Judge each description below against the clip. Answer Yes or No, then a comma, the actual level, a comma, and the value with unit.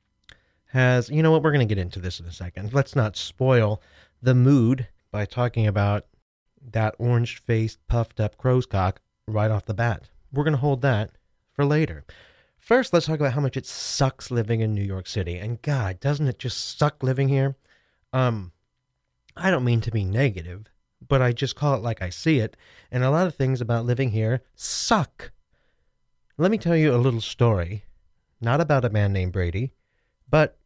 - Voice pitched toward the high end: No, low, 120 Hz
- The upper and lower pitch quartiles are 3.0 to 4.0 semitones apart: No, average, 4.9 semitones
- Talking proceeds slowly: No, average, 190 wpm